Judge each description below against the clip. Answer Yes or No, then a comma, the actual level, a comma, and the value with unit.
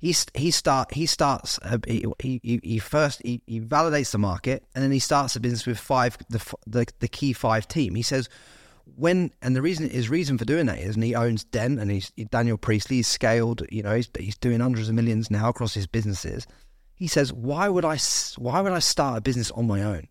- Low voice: Yes, low, 120 Hz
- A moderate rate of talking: No, fast, 225 wpm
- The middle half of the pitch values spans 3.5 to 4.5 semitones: Yes, average, 3.8 semitones